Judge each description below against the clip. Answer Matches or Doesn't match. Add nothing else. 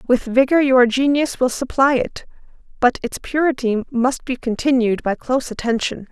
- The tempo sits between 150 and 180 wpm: Matches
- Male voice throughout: Doesn't match